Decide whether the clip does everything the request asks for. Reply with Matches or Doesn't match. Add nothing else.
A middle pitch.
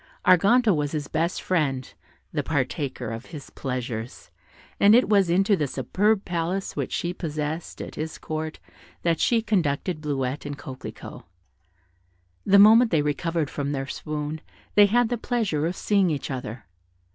Matches